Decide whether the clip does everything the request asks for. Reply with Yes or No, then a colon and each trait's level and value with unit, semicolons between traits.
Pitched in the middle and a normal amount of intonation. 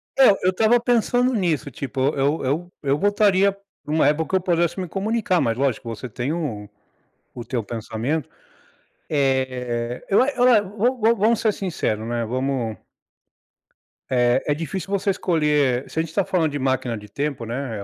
No: medium, 150 Hz; wide, 7.5 semitones